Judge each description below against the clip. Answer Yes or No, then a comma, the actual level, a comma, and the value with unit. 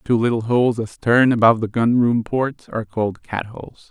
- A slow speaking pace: No, average, 200 wpm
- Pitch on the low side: Yes, low, 115 Hz